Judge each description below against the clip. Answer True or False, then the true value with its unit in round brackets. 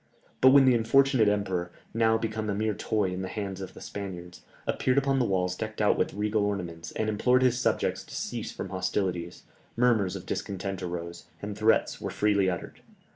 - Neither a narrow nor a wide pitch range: True (3.2 semitones)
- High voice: False (105 Hz)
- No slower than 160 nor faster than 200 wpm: True (190 wpm)